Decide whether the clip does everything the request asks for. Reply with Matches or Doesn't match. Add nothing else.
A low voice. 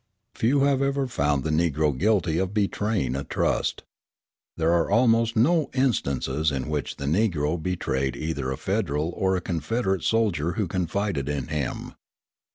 Matches